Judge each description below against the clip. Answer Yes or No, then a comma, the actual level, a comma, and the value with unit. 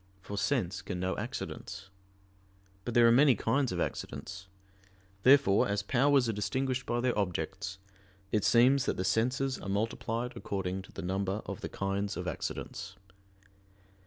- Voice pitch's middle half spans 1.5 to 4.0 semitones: No, average, 4.5 semitones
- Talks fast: No, average, 155 wpm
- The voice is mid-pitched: No, low, 105 Hz